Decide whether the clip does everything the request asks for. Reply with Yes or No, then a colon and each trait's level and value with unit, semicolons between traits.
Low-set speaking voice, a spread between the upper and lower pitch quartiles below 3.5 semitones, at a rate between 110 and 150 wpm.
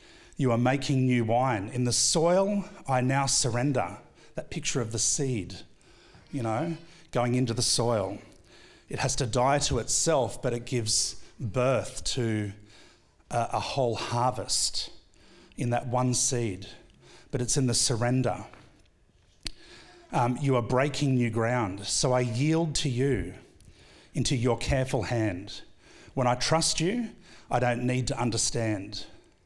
Yes: low, 125 Hz; average, 3.1 semitones; average, 145 wpm